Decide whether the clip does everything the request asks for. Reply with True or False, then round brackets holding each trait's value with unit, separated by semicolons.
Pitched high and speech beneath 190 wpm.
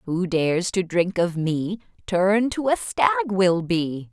True (195 Hz; 175 wpm)